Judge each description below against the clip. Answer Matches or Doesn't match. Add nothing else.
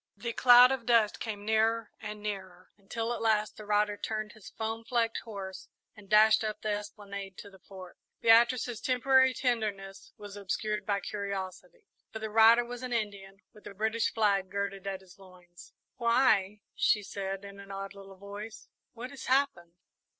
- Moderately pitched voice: Doesn't match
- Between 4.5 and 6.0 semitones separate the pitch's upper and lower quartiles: Doesn't match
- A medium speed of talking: Matches